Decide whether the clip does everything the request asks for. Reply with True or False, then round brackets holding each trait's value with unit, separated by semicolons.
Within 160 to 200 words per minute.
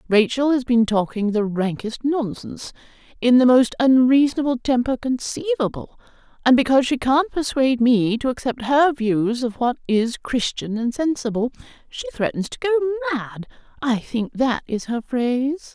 False (150 wpm)